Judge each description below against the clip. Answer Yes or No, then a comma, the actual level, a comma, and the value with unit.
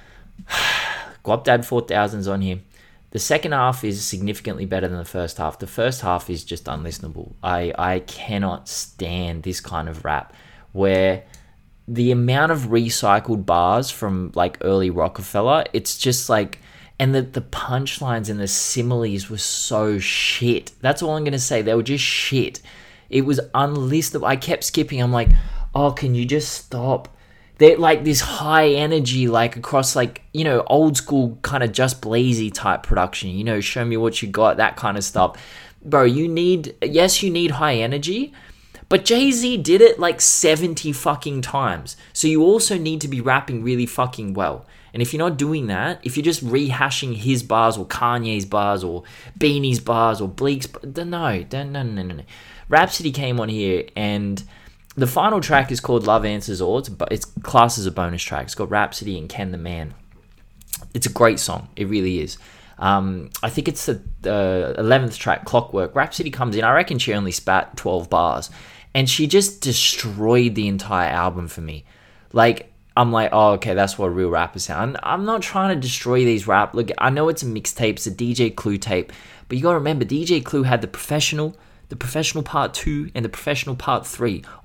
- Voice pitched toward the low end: Yes, low, 120 Hz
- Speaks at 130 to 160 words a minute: No, average, 190 wpm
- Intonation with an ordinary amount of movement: No, wide, 6.0 semitones